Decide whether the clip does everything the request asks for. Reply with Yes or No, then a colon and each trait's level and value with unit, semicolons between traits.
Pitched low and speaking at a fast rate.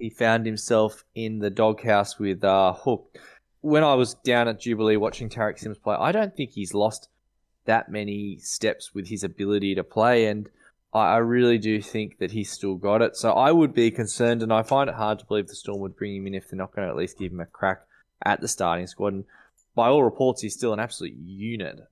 Yes: low, 110 Hz; fast, 225 wpm